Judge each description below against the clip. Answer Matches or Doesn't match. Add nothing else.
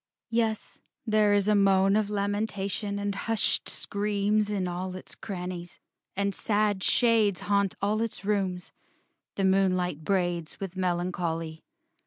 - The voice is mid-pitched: Doesn't match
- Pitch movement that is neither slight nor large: Doesn't match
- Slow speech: Matches